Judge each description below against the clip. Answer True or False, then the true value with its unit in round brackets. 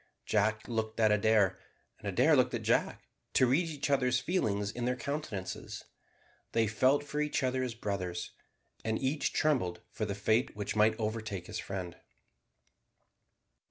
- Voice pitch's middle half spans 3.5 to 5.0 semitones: True (4.1 semitones)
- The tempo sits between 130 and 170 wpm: True (155 wpm)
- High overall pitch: False (110 Hz)